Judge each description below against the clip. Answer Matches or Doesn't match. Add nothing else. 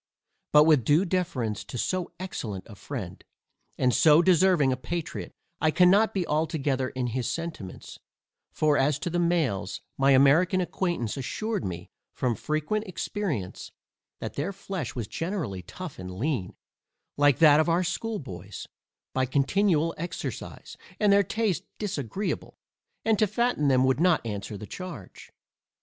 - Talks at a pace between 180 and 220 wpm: Doesn't match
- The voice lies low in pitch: Doesn't match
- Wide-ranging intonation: Matches